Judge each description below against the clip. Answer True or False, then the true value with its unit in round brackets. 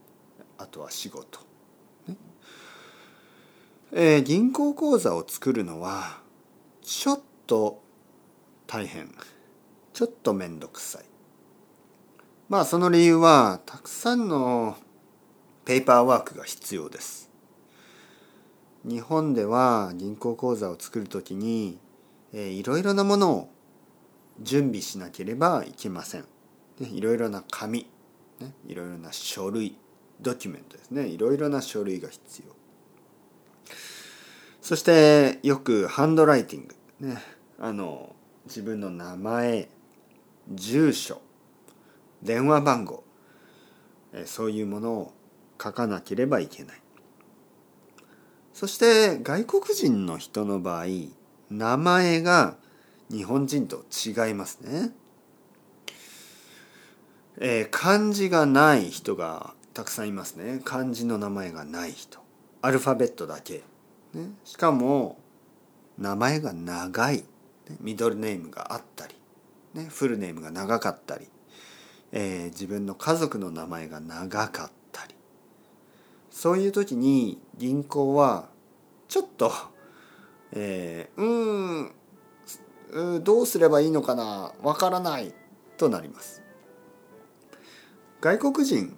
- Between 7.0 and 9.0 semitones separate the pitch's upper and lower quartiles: True (8.0 semitones)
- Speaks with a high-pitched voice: False (130 Hz)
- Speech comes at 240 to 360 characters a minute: False (215 characters per minute)